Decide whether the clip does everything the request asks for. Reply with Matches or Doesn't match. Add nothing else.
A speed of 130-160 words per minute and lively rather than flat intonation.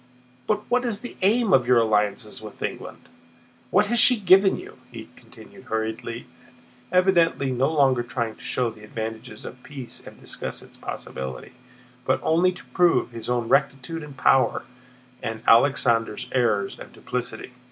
Matches